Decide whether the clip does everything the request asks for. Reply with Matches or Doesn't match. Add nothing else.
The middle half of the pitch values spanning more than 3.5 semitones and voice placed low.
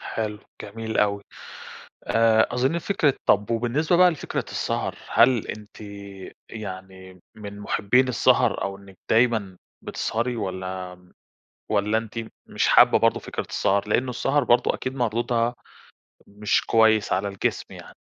Doesn't match